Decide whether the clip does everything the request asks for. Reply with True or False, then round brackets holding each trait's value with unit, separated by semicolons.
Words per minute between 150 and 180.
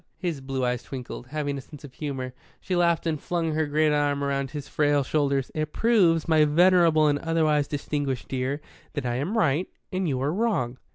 False (195 wpm)